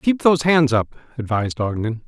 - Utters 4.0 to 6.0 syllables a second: Yes, 5.5 syllables/s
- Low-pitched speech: Yes, low, 130 Hz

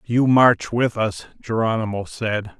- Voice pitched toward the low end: Yes, low, 115 Hz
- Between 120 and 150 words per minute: Yes, average, 140 wpm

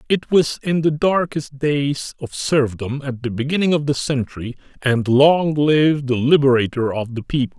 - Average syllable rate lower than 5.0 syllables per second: Yes, 4.6 syllables/s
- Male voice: Yes, male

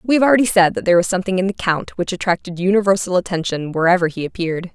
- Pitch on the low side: No, medium, 185 Hz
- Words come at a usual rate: No, fast, 230 wpm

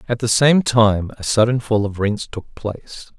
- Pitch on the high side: No, low, 115 Hz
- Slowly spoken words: No, fast, 205 wpm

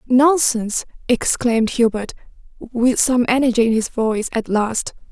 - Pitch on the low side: No, high, 240 Hz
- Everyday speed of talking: No, slow, 130 wpm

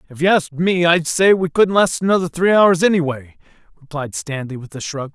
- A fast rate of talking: Yes, fast, 210 wpm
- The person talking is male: Yes, male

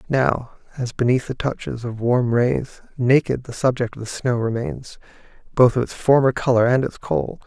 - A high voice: No, low, 125 Hz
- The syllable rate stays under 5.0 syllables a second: Yes, 4.8 syllables/s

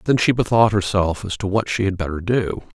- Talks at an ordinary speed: No, fast, 235 wpm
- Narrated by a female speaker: No, male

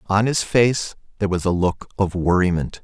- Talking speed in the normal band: Yes, average, 190 wpm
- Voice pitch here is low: Yes, very low, 95 Hz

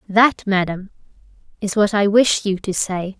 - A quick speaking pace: No, average, 170 wpm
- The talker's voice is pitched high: Yes, high, 200 Hz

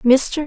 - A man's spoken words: No, female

